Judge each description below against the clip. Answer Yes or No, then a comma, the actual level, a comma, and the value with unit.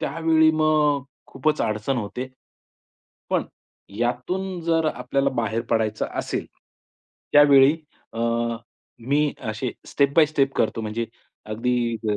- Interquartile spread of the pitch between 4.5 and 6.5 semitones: Yes, average, 5.2 semitones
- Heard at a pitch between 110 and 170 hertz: Yes, low, 135 Hz